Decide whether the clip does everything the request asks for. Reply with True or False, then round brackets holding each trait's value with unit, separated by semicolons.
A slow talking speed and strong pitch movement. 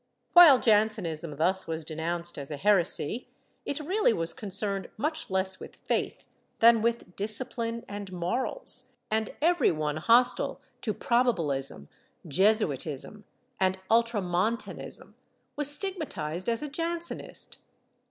True (115 wpm; 6.1 semitones)